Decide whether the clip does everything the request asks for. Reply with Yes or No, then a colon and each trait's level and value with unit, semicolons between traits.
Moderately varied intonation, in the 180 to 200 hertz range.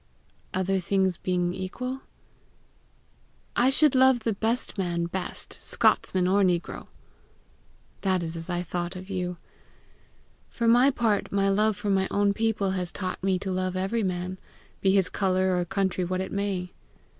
No: narrow, 2.1 semitones; high, 190 Hz